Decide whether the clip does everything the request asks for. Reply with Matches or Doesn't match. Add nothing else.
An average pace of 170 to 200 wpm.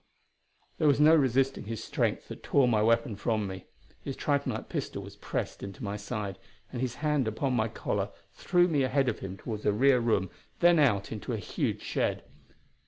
Matches